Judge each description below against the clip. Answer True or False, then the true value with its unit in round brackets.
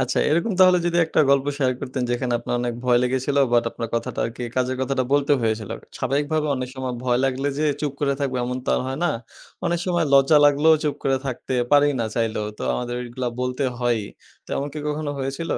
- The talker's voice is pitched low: True (130 Hz)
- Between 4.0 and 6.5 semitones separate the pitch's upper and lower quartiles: False (2.9 semitones)